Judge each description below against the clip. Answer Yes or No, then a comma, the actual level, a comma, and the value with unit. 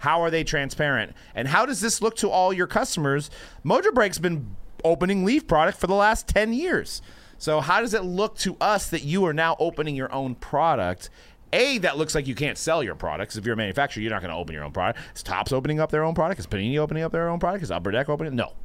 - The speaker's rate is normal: No, fast, 255 wpm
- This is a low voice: No, medium, 155 Hz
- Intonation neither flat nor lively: No, wide, 6.1 semitones